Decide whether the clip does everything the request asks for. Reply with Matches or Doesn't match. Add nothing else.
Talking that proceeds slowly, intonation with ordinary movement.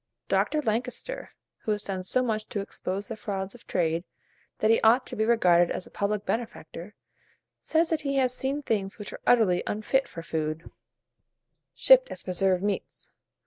Doesn't match